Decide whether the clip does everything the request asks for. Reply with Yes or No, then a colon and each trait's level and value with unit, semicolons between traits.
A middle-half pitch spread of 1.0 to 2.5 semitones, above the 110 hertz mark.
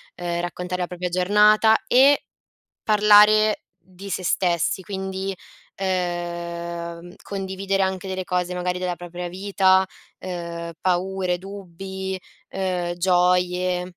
Yes: narrow, 1.5 semitones; medium, 185 Hz